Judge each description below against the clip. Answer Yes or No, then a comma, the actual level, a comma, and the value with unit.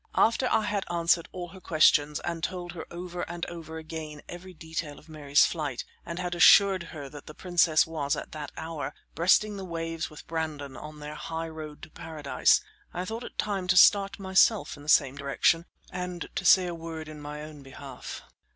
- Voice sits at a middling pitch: Yes, medium, 165 Hz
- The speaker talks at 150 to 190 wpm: No, average, 200 wpm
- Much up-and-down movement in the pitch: No, average, 2.8 semitones